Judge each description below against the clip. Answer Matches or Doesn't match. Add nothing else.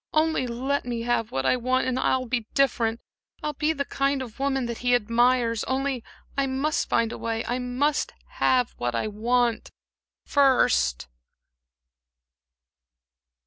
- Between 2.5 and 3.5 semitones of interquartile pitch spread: Matches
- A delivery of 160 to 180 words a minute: Doesn't match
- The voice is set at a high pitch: Matches